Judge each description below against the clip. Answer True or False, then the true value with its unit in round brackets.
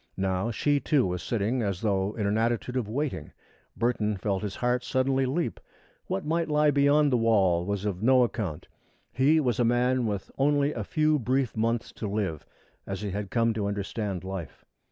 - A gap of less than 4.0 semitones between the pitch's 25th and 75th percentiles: False (4.7 semitones)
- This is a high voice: False (115 Hz)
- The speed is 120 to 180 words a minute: False (190 wpm)